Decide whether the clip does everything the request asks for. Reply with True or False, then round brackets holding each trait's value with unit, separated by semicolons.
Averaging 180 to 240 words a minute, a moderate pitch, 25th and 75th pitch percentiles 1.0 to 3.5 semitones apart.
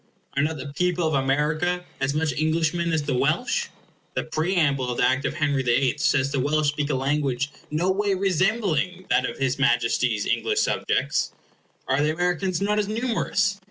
False (185 wpm; 150 Hz; 4.6 semitones)